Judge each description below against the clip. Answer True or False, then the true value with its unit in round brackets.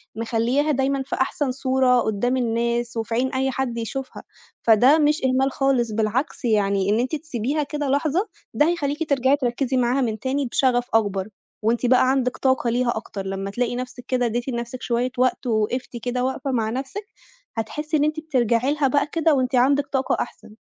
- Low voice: False (255 Hz)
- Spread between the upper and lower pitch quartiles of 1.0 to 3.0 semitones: True (2.7 semitones)